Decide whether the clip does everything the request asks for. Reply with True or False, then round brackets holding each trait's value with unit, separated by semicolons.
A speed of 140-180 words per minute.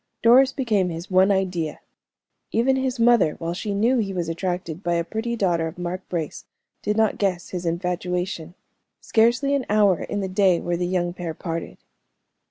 True (175 wpm)